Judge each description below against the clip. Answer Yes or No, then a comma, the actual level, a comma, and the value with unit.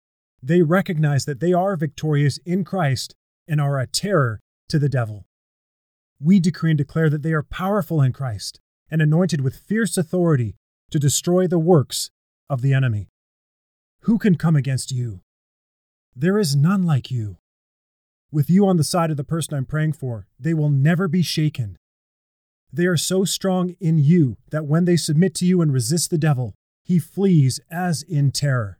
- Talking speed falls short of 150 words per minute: No, average, 175 wpm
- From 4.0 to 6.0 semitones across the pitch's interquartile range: Yes, wide, 5.6 semitones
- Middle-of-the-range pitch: Yes, medium, 150 Hz